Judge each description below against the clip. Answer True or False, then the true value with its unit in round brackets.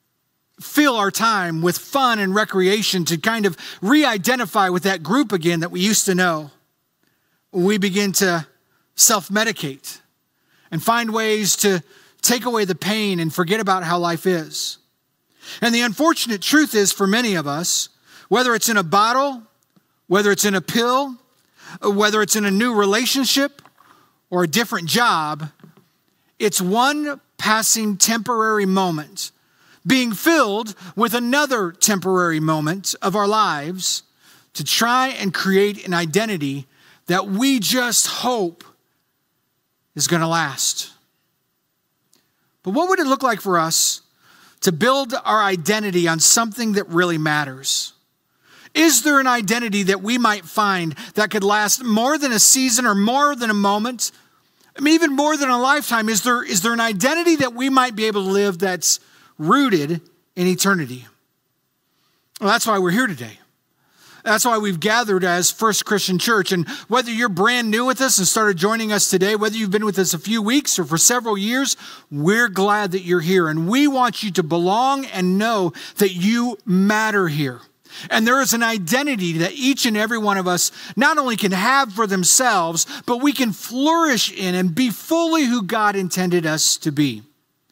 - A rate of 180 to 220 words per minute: False (170 wpm)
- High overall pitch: True (210 Hz)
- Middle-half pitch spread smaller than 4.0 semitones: False (4.8 semitones)